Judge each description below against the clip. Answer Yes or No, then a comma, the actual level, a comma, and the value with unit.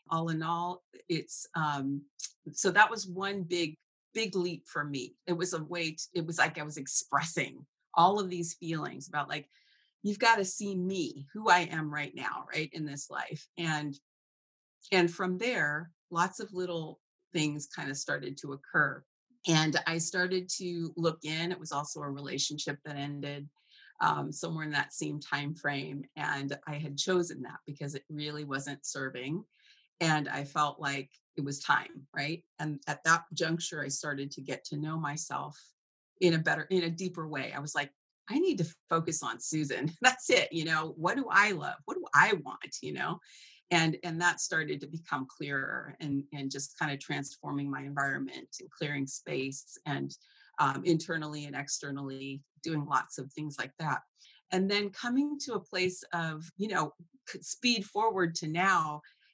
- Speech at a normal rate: Yes, average, 180 wpm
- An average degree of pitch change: Yes, average, 3.5 semitones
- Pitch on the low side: No, medium, 160 Hz